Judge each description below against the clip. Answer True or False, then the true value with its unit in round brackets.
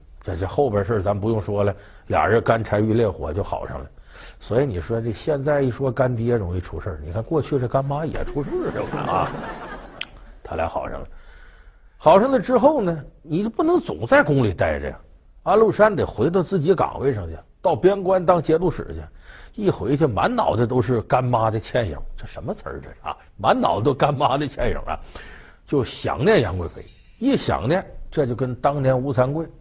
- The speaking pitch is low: True (125 Hz)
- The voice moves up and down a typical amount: False (7.7 semitones)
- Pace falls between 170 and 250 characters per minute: False (280 characters per minute)